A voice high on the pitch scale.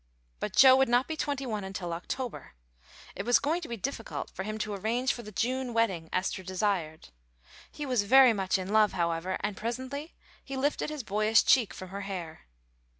Yes: high, 215 Hz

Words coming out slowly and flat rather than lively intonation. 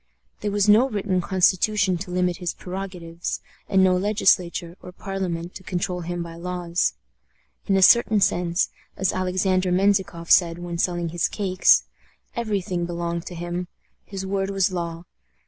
No: average, 155 wpm; narrow, 1.9 semitones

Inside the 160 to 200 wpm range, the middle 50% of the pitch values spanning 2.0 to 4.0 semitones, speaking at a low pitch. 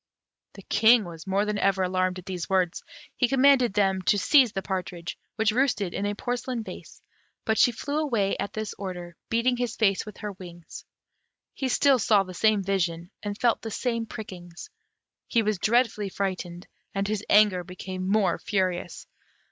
No: average, 175 wpm; average, 3.6 semitones; high, 205 Hz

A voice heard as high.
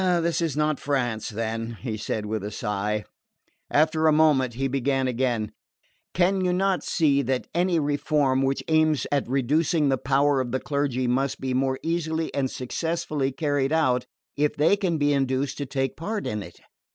No: medium, 140 Hz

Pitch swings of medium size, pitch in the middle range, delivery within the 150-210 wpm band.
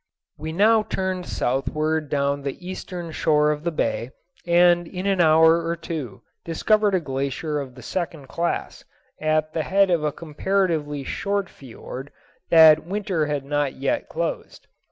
Yes: average, 3.4 semitones; medium, 160 Hz; average, 155 wpm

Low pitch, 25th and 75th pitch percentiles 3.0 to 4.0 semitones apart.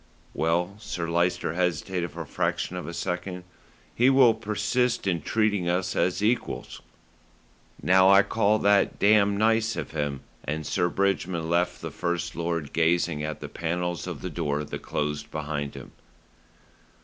Yes: very low, 90 Hz; average, 3.5 semitones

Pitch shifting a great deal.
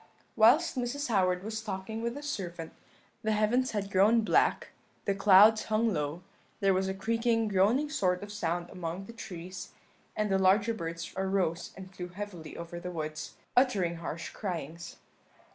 No: average, 3.8 semitones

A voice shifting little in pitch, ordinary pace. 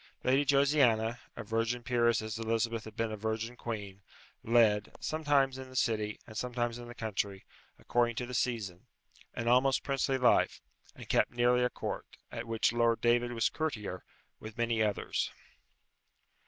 Yes: narrow, 2.0 semitones; average, 160 wpm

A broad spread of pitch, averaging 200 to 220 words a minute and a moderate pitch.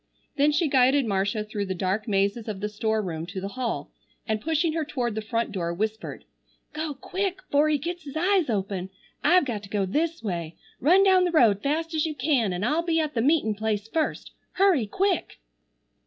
No: wide, 7.5 semitones; fast, 205 wpm; high, 245 Hz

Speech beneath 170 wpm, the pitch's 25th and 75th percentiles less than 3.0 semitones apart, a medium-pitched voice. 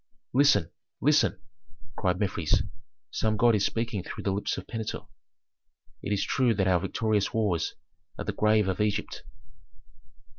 No: average, 145 wpm; narrow, 2.6 semitones; low, 105 Hz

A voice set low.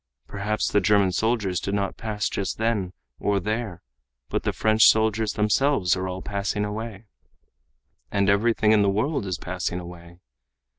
Yes: low, 105 Hz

